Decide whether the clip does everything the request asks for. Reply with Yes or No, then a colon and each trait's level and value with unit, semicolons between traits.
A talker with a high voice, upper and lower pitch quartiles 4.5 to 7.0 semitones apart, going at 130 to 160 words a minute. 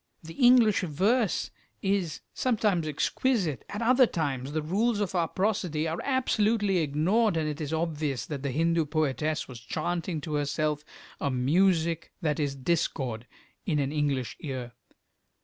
No: medium, 160 Hz; average, 5.1 semitones; average, 150 wpm